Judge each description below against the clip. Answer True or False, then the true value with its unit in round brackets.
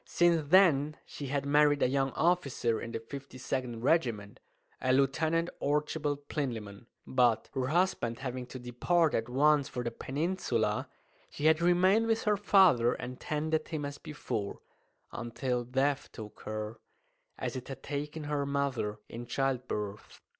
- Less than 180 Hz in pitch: True (140 Hz)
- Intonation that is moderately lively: True (4.1 semitones)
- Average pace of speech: True (145 wpm)